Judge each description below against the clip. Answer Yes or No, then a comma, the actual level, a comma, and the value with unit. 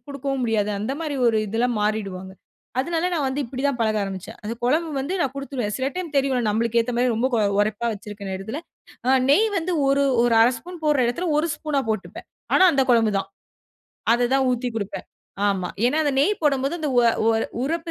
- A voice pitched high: Yes, very high, 250 Hz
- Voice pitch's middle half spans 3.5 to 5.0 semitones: Yes, average, 4.7 semitones